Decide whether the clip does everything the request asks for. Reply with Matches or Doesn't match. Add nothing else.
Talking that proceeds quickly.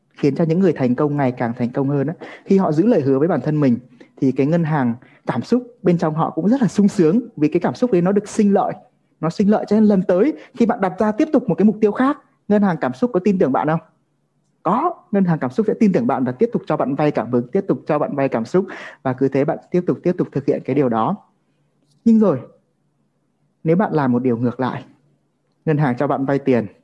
Matches